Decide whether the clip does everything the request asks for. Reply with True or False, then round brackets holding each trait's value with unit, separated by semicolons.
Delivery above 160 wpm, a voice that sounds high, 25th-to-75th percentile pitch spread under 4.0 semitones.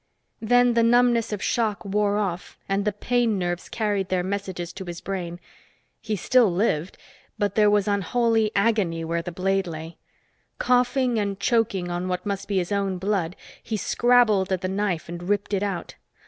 True (175 wpm; 200 Hz; 3.3 semitones)